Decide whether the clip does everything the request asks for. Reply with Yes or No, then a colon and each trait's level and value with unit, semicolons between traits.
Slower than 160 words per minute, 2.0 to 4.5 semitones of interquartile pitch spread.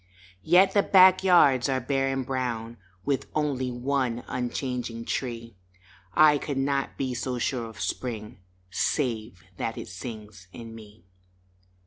Yes: slow, 135 wpm; average, 3.2 semitones